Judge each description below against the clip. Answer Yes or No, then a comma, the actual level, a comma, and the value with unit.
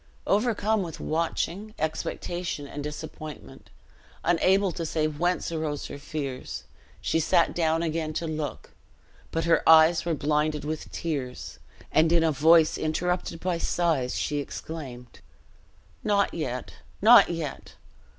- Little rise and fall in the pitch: Yes, narrow, 2.3 semitones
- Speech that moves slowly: Yes, slow, 130 wpm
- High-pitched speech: No, medium, 160 Hz